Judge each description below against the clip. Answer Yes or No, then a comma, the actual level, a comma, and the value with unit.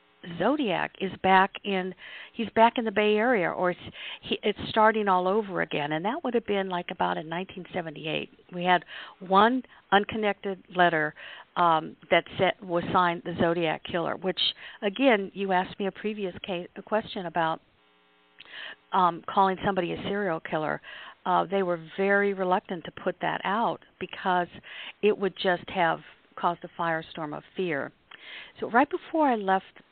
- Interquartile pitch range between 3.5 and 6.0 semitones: No, average, 2.8 semitones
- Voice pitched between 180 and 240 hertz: Yes, medium, 185 Hz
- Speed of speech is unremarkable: Yes, average, 160 wpm